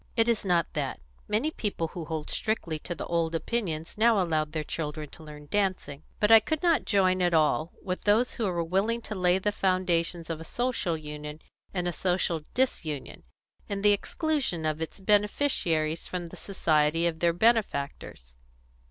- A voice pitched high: No, medium, 175 Hz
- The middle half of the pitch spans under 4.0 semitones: No, average, 4.8 semitones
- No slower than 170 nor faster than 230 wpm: Yes, average, 180 wpm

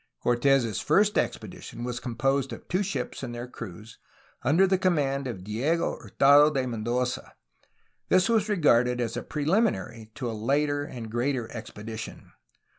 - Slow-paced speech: No, average, 150 wpm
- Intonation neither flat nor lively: Yes, average, 4.3 semitones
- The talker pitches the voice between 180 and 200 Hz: No, low, 130 Hz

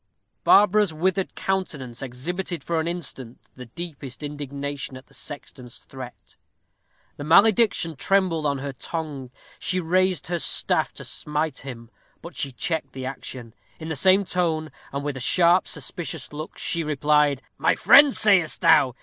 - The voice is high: No, medium, 155 Hz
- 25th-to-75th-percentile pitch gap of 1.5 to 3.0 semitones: No, average, 4.7 semitones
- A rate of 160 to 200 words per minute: No, average, 150 wpm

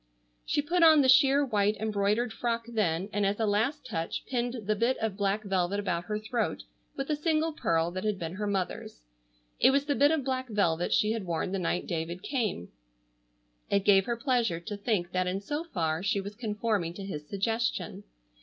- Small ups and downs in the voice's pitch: No, average, 4.7 semitones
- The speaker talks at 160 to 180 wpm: No, average, 200 wpm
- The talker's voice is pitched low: No, high, 210 Hz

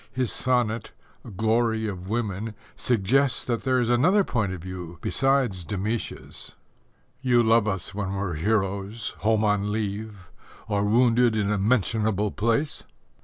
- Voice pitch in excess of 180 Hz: No, low, 110 Hz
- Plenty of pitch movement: No, average, 3.2 semitones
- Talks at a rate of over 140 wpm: No, slow, 135 wpm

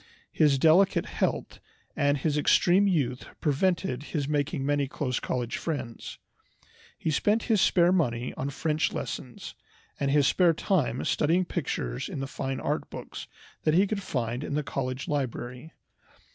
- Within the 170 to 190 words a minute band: No, average, 150 wpm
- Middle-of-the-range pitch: Yes, medium, 145 Hz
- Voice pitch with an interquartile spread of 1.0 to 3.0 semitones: No, average, 4.4 semitones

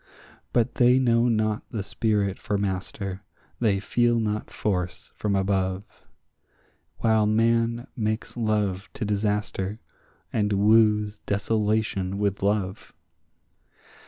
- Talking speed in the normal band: No, slow, 105 wpm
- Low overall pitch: Yes, low, 105 Hz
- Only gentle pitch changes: Yes, narrow, 2.1 semitones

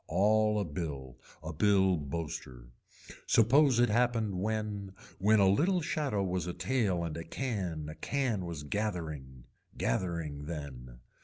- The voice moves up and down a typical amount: No, wide, 5.8 semitones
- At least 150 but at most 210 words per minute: No, average, 140 wpm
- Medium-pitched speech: No, very low, 95 Hz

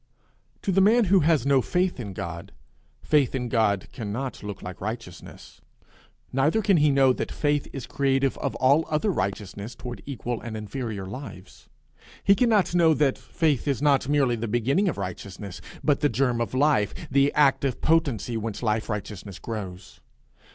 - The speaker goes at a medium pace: Yes, average, 165 wpm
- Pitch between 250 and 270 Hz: No, low, 130 Hz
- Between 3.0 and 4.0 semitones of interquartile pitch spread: No, wide, 5.6 semitones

